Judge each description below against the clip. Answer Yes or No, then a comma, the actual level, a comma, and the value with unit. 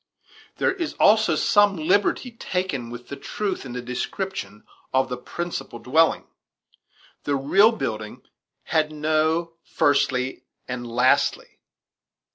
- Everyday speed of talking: No, slow, 115 wpm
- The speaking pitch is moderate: Yes, medium, 155 Hz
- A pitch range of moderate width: No, wide, 7.3 semitones